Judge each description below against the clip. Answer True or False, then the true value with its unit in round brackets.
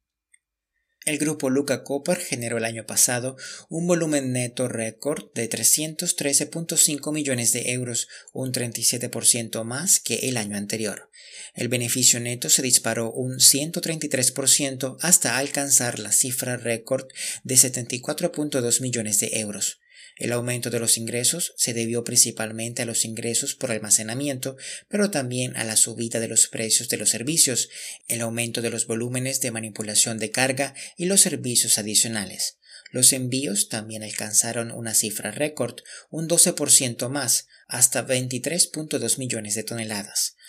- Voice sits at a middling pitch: False (125 Hz)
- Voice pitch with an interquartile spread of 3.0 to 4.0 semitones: True (3.5 semitones)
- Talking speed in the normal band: True (140 wpm)